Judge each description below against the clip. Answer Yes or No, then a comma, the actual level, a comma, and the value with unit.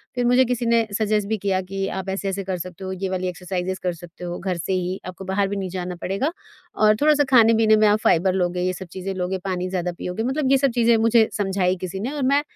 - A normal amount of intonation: Yes, average, 3.3 semitones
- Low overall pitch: No, high, 195 Hz